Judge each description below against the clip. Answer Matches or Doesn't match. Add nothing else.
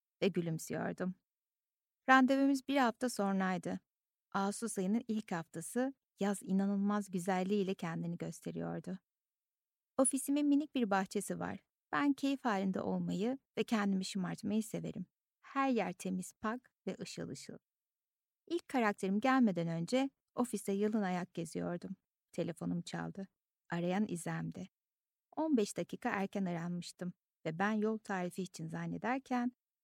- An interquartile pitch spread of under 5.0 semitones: Doesn't match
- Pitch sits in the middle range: Doesn't match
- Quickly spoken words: Doesn't match